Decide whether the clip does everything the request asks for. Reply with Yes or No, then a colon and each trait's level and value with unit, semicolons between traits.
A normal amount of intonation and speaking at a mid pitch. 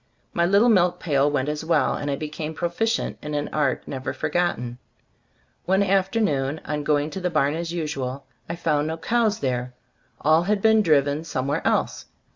Yes: average, 3.8 semitones; medium, 155 Hz